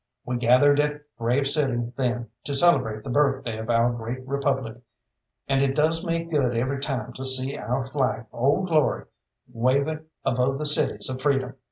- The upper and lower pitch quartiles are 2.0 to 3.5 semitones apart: Yes, average, 2.9 semitones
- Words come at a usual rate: Yes, average, 170 wpm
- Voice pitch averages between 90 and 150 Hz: Yes, low, 135 Hz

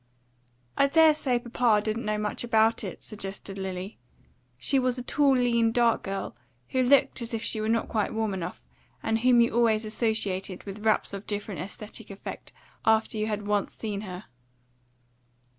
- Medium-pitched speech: No, high, 220 Hz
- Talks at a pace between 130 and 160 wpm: No, average, 175 wpm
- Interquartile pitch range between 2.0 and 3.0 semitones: Yes, narrow, 2.6 semitones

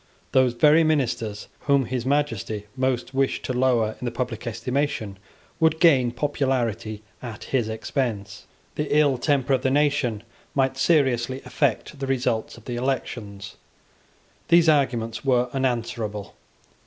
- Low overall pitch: Yes, low, 125 Hz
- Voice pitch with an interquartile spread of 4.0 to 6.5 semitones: No, average, 3.3 semitones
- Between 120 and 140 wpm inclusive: Yes, slow, 135 wpm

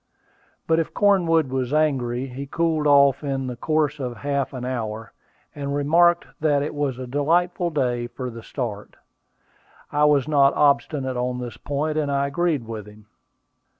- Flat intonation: No, average, 3.3 semitones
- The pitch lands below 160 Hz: Yes, medium, 140 Hz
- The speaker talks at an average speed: Yes, average, 165 wpm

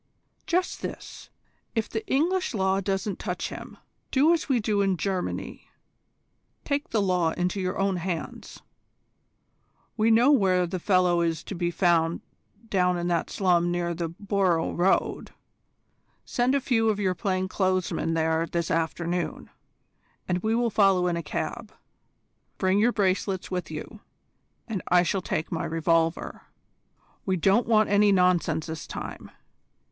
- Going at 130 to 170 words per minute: Yes, average, 150 wpm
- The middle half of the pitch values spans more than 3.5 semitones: No, average, 3.2 semitones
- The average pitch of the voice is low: No, medium, 185 Hz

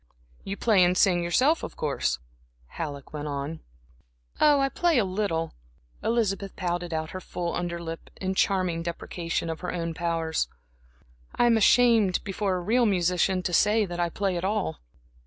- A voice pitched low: No, medium, 180 Hz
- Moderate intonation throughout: Yes, average, 3.6 semitones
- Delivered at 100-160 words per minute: No, average, 170 wpm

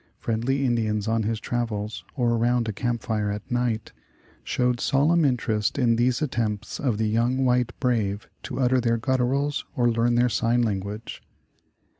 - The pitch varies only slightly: Yes, narrow, 2.1 semitones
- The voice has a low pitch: Yes, low, 120 Hz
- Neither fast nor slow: Yes, average, 170 wpm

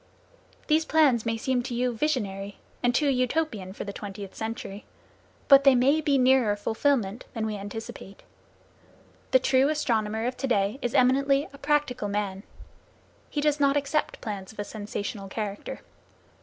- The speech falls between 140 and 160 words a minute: Yes, average, 155 wpm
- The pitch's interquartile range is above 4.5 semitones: Yes, average, 5.1 semitones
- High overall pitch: Yes, high, 245 Hz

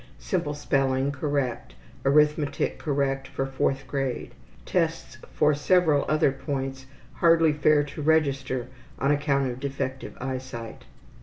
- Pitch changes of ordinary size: No, narrow, 1.9 semitones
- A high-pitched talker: No, medium, 140 Hz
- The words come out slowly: Yes, slow, 120 wpm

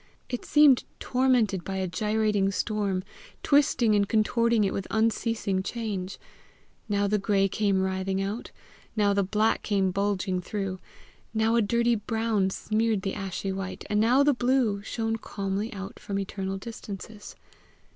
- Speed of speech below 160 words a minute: Yes, average, 145 wpm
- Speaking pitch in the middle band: No, high, 205 Hz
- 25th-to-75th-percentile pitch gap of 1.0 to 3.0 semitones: Yes, narrow, 2.6 semitones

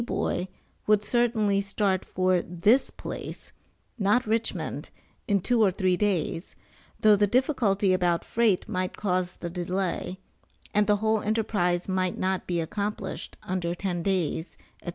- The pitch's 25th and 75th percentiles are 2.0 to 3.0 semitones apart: Yes, average, 2.7 semitones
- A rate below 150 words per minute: Yes, slow, 135 wpm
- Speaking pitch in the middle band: No, high, 195 Hz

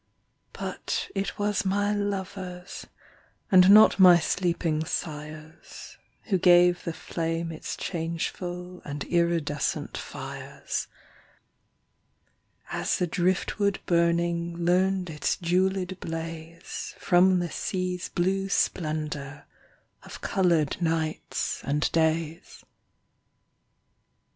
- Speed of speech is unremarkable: No, slow, 90 wpm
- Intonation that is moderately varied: No, narrow, 2.3 semitones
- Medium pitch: Yes, medium, 175 Hz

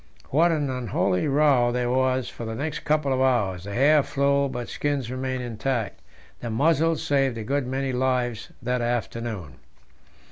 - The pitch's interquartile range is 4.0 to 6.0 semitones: No, average, 2.8 semitones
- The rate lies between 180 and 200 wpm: No, average, 165 wpm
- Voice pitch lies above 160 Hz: No, low, 130 Hz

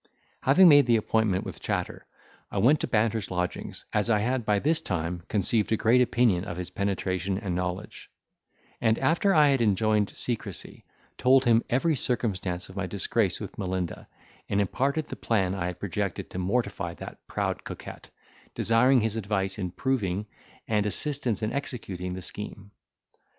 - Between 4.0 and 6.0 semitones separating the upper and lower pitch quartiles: Yes, average, 4.5 semitones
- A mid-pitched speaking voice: No, low, 105 Hz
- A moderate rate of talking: Yes, average, 165 wpm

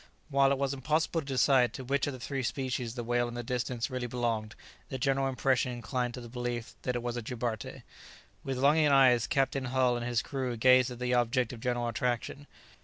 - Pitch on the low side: Yes, low, 125 Hz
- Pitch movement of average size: No, narrow, 1.8 semitones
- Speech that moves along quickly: Yes, fast, 215 wpm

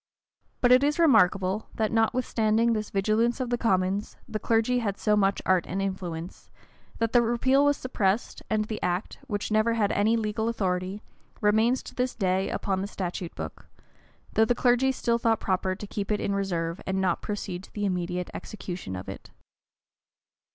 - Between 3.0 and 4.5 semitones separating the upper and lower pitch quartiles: Yes, average, 3.4 semitones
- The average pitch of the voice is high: Yes, high, 210 Hz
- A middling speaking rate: Yes, average, 180 wpm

